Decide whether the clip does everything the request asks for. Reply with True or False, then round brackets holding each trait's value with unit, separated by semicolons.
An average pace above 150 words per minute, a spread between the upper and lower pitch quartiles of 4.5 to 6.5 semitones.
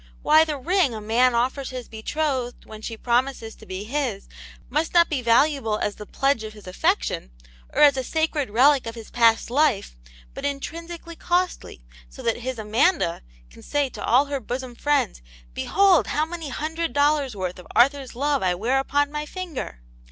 True (185 wpm; 4.9 semitones)